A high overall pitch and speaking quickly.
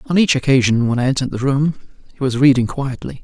No: low, 135 Hz; fast, 225 wpm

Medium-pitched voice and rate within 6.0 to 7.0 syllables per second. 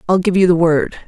Yes: medium, 175 Hz; 6.1 syllables/s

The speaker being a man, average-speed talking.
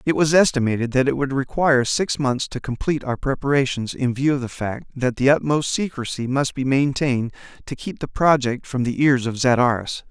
No: male; fast, 210 wpm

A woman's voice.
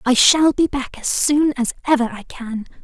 Yes: female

